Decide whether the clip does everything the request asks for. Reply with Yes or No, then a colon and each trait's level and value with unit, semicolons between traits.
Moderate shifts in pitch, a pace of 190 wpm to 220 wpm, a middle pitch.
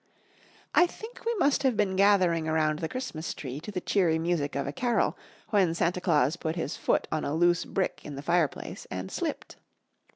Yes: average, 4.4 semitones; average, 195 wpm; medium, 170 Hz